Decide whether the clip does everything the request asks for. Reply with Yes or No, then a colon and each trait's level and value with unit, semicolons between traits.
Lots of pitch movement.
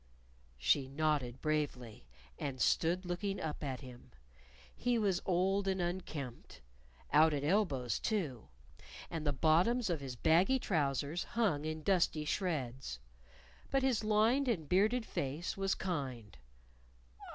Yes: wide, 5.9 semitones